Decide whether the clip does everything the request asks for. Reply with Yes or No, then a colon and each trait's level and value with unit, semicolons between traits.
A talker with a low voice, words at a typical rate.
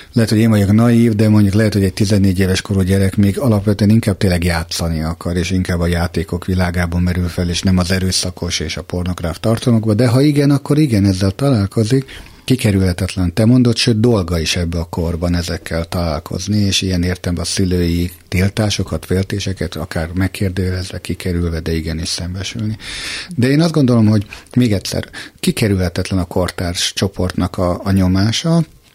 No: very low, 95 Hz; fast, 165 wpm